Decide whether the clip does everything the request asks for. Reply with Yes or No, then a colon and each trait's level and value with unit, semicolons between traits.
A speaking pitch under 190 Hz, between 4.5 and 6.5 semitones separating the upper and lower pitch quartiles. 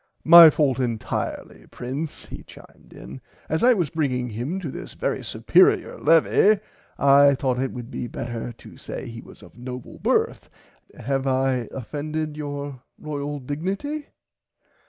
No: medium, 140 Hz; average, 3.7 semitones